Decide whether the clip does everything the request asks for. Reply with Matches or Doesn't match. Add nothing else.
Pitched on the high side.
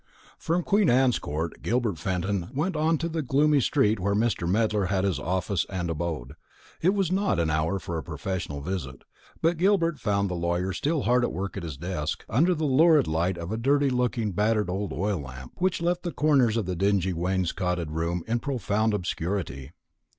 Doesn't match